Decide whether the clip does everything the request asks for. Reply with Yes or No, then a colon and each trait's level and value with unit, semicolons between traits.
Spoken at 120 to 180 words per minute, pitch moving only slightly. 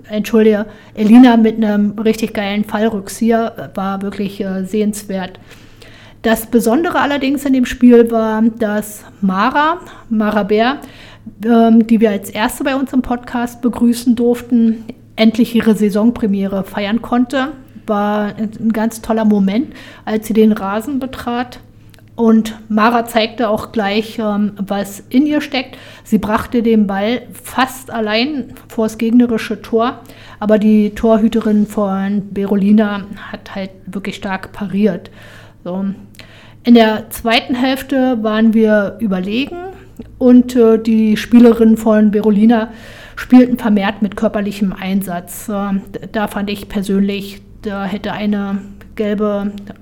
Yes: slow, 125 wpm; narrow, 2.3 semitones